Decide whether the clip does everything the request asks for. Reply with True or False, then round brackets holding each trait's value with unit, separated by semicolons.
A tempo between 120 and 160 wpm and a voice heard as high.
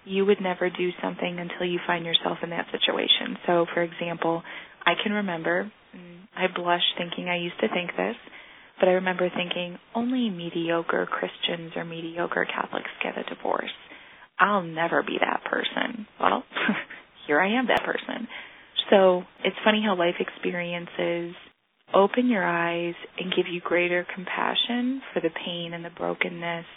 False (155 wpm; 175 Hz)